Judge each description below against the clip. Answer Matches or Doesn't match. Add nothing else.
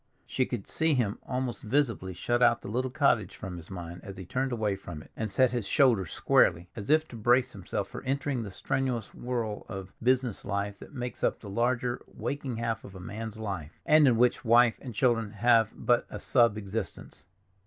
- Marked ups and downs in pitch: Doesn't match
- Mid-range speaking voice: Doesn't match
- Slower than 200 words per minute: Doesn't match